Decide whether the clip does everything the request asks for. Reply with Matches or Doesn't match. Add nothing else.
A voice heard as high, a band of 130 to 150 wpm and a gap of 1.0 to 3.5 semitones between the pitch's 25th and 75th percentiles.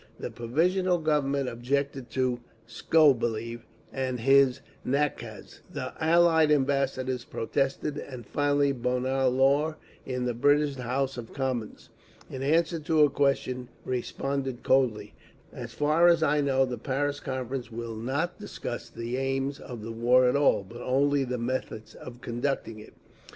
Doesn't match